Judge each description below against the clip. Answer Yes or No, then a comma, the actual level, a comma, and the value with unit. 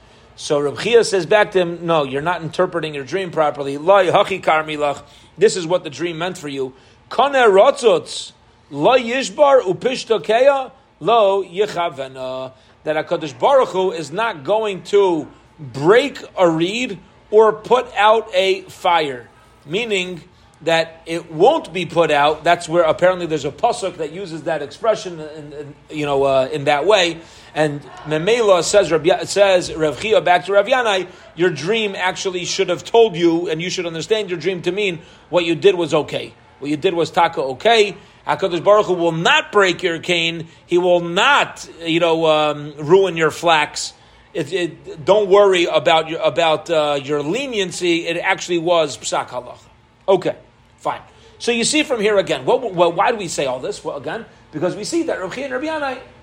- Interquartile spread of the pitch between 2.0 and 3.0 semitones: No, average, 4.5 semitones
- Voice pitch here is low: No, medium, 175 Hz